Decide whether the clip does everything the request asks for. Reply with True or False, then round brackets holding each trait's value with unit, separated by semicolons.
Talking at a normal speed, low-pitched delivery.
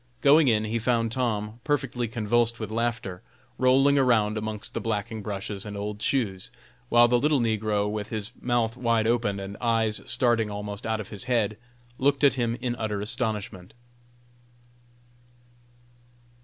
True (150 wpm; 110 Hz)